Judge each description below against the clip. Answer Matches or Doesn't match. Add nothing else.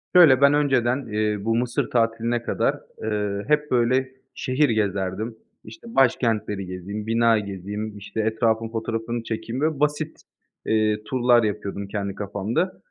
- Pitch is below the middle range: Matches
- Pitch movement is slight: Doesn't match